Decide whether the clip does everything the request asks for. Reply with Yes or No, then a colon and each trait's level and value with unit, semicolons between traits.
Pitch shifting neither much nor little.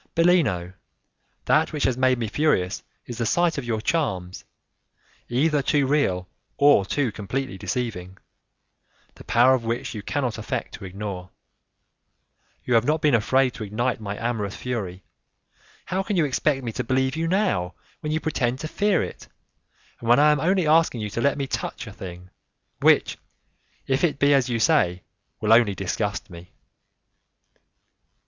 No: wide, 6.0 semitones